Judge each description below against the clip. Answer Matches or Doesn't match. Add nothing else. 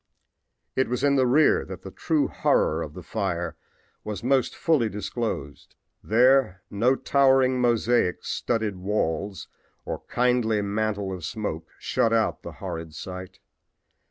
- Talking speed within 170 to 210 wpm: Doesn't match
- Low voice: Matches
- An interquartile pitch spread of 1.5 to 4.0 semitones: Doesn't match